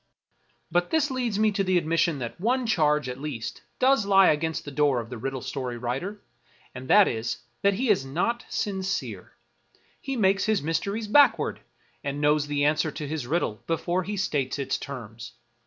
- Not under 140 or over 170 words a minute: No, average, 180 wpm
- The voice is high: No, medium, 160 Hz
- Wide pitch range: Yes, wide, 6.5 semitones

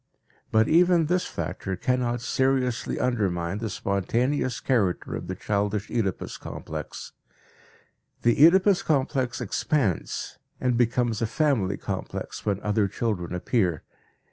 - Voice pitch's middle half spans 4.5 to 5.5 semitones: Yes, average, 4.8 semitones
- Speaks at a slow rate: Yes, slow, 115 wpm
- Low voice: Yes, low, 115 Hz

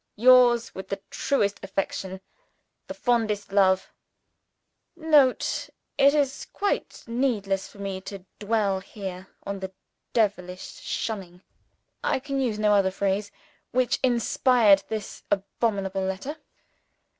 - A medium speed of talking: No, slow, 120 wpm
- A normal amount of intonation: Yes, average, 4.1 semitones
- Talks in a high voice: Yes, high, 205 Hz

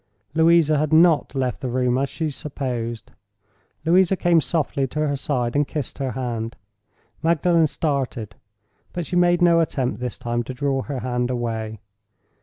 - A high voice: No, low, 135 Hz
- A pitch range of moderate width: Yes, average, 4.7 semitones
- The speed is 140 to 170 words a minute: Yes, average, 155 wpm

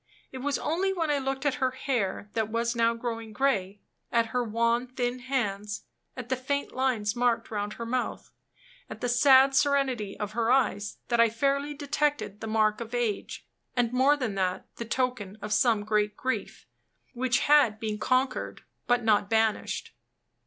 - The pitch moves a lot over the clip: No, average, 3.4 semitones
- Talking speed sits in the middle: Yes, average, 175 wpm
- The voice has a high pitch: Yes, high, 240 Hz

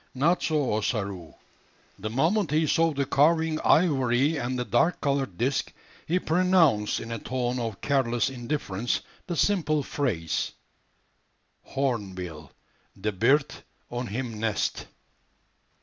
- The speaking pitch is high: No, low, 130 Hz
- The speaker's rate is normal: No, slow, 120 wpm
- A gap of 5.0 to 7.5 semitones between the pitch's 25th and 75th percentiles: Yes, wide, 5.4 semitones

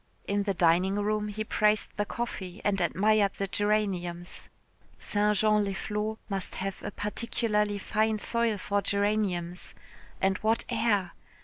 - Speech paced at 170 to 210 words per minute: No, average, 140 wpm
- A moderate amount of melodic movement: No, narrow, 1.8 semitones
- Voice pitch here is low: No, high, 205 Hz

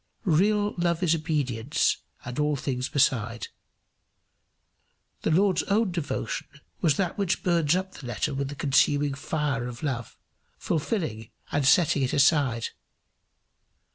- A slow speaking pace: Yes, slow, 130 wpm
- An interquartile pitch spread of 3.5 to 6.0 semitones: Yes, average, 4.5 semitones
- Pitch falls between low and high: Yes, medium, 145 Hz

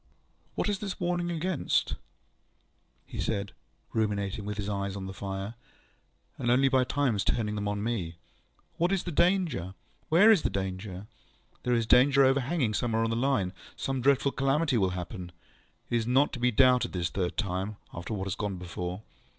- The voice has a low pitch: Yes, low, 115 Hz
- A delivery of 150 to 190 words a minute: Yes, average, 175 wpm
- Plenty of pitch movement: Yes, wide, 5.9 semitones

